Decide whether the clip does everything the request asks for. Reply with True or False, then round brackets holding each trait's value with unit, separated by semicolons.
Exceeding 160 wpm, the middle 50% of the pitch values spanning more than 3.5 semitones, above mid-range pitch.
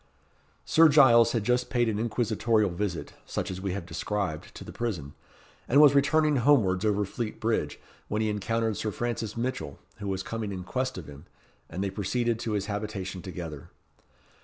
False (180 wpm; 3.9 semitones; 105 Hz)